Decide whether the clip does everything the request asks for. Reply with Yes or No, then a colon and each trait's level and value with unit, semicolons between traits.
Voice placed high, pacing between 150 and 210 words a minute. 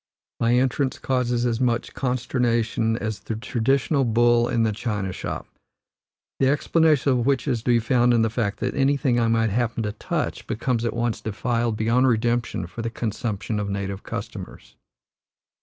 No: low, 120 Hz; average, 170 wpm